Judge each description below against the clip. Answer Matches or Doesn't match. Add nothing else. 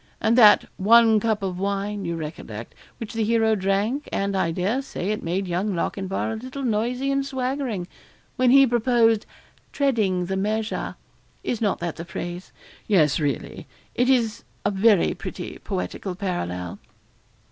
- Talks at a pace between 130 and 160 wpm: Matches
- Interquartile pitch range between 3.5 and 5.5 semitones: Matches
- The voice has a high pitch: Matches